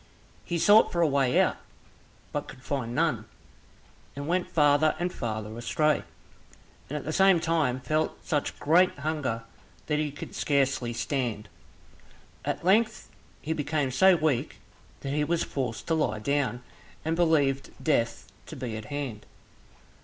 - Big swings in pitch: No, average, 4.2 semitones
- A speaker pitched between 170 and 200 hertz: No, medium, 145 Hz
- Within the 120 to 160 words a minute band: Yes, average, 155 wpm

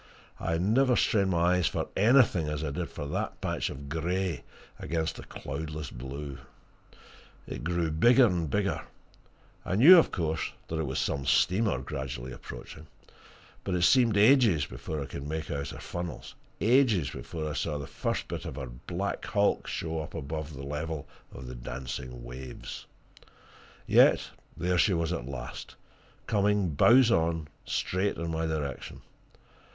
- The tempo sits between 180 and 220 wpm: No, average, 160 wpm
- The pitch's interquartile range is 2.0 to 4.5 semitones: No, average, 5.1 semitones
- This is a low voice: Yes, very low, 80 Hz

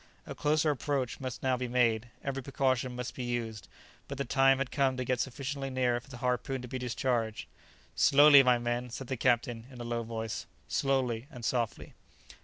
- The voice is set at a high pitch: No, low, 125 Hz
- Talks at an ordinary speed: Yes, average, 195 wpm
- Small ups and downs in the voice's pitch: Yes, narrow, 2.1 semitones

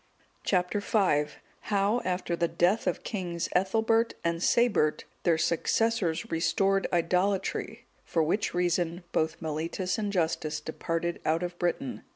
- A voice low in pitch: No, medium, 175 Hz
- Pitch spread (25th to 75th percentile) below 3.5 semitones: Yes, average, 3.0 semitones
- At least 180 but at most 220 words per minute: No, average, 140 wpm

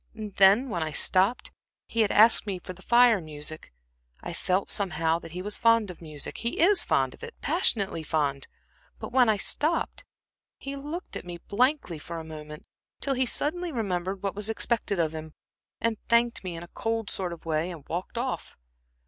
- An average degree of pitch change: No, wide, 6.1 semitones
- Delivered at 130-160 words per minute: No, average, 195 wpm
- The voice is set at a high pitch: Yes, high, 195 Hz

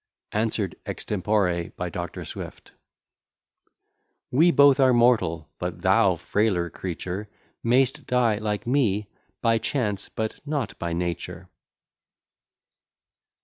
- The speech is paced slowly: Yes, slow, 105 wpm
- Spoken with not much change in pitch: No, average, 5.2 semitones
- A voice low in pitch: Yes, low, 105 Hz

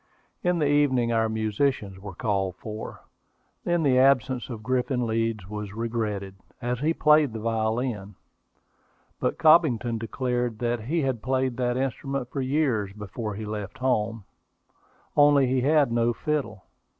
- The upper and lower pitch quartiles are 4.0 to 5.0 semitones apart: No, average, 3.6 semitones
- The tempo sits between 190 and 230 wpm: No, average, 145 wpm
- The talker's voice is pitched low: Yes, low, 120 Hz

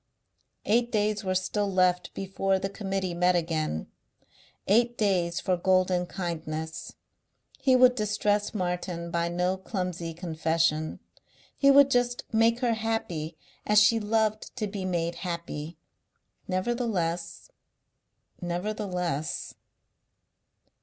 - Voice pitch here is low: No, medium, 185 Hz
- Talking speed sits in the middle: No, slow, 110 wpm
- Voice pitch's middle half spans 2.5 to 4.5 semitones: Yes, average, 3.8 semitones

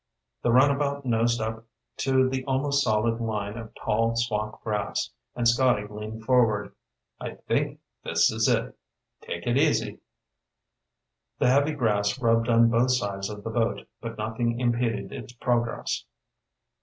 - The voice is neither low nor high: No, low, 115 Hz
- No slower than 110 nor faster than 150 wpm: Yes, average, 145 wpm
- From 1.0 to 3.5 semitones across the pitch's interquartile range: Yes, narrow, 2.5 semitones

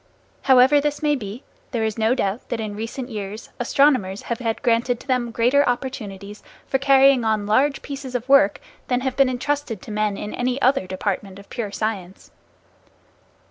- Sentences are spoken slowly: No, average, 180 wpm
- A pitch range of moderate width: Yes, average, 4.1 semitones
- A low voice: No, high, 240 Hz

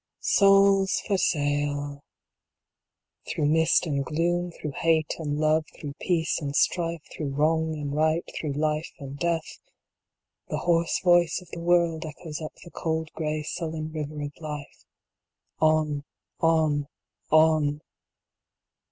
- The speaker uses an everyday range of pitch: No, narrow, 2.0 semitones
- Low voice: No, medium, 155 Hz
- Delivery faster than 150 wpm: No, slow, 135 wpm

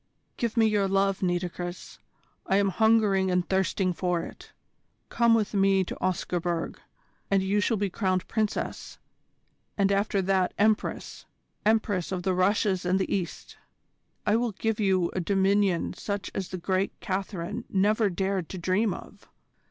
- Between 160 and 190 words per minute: No, average, 150 wpm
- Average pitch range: No, narrow, 2.0 semitones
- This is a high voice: Yes, high, 195 Hz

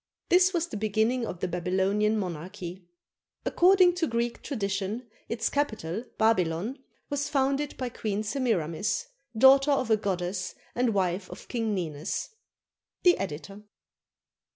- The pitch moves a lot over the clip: Yes, wide, 6.1 semitones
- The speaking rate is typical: No, slow, 130 wpm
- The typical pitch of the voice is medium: No, high, 215 Hz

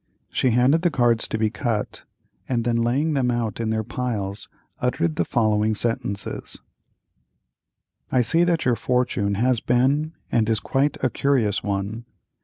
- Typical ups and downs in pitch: Yes, average, 3.0 semitones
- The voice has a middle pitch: No, low, 120 Hz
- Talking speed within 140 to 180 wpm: Yes, average, 155 wpm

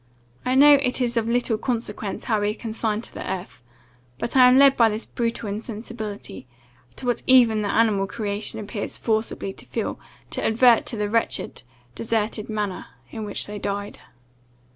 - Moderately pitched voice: No, high, 220 Hz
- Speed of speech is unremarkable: Yes, average, 175 wpm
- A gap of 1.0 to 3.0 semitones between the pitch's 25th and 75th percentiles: Yes, narrow, 2.4 semitones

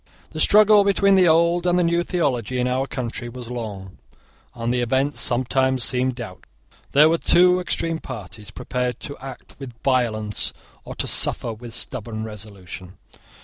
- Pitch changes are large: Yes, wide, 6.0 semitones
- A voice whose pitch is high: No, low, 125 Hz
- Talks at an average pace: Yes, average, 160 wpm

